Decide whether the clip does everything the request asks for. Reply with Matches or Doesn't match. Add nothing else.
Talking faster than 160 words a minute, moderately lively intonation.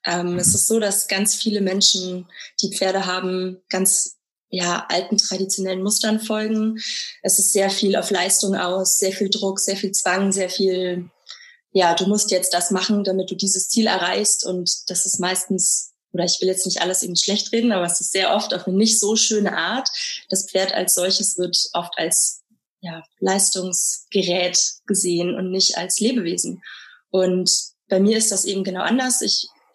Doesn't match